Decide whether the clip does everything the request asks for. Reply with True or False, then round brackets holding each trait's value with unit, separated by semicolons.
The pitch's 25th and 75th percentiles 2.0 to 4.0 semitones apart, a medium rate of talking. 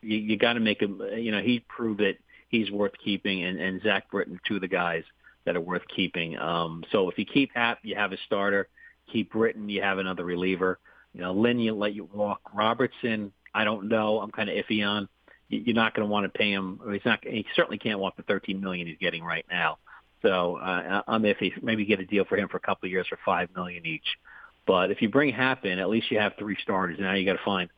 False (2.8 semitones; 255 wpm)